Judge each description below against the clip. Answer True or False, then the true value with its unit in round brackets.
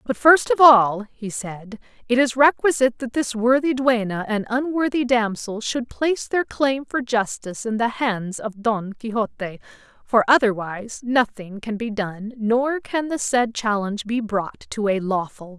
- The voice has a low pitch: False (235 Hz)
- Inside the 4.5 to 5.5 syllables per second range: True (4.6 syllables/s)